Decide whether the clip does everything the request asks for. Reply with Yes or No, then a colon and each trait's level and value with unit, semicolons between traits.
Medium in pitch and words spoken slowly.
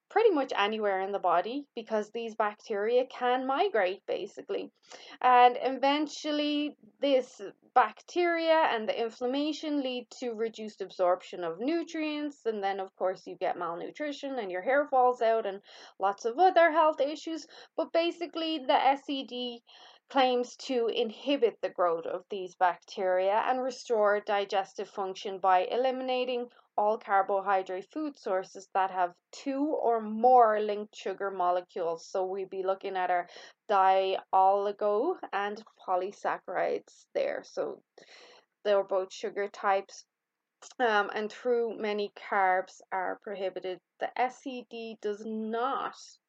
No: high, 225 Hz; slow, 130 wpm